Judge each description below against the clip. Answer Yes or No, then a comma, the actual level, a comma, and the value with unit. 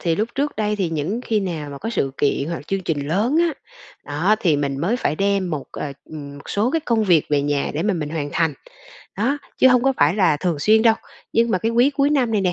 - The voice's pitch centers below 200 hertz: Yes, high, 190 Hz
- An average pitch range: No, wide, 7.0 semitones